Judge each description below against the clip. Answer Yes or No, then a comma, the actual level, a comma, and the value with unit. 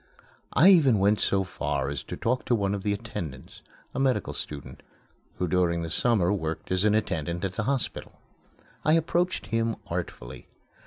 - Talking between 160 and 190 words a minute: Yes, average, 170 wpm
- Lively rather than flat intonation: Yes, wide, 5.7 semitones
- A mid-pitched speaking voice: No, low, 100 Hz